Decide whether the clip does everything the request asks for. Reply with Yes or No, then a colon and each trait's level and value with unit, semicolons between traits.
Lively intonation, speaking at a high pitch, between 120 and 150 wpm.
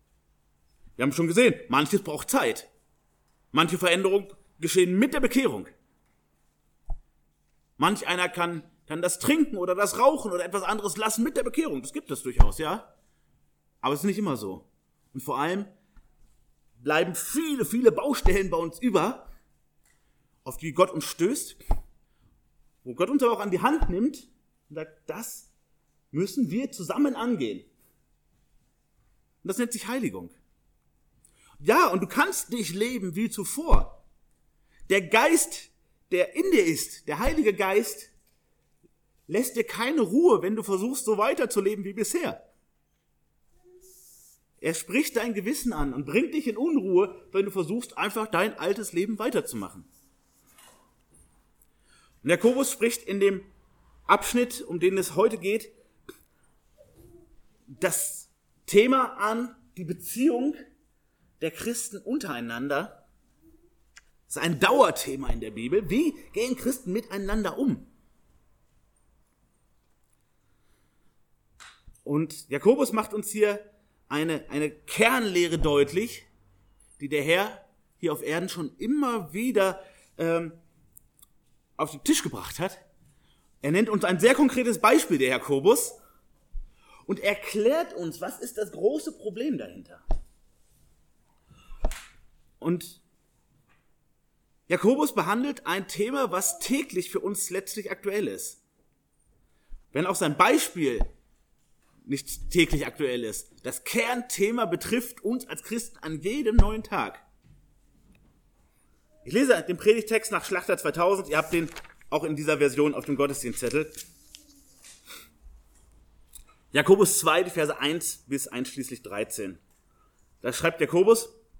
Yes: wide, 7.0 semitones; high, 200 Hz; slow, 125 wpm